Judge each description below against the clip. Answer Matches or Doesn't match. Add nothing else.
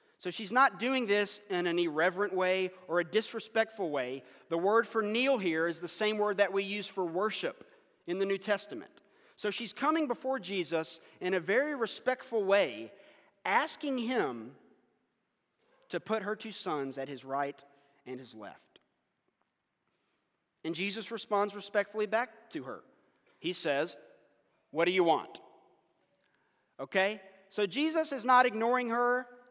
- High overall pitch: Matches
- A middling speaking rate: Matches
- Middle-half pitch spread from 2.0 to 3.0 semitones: Doesn't match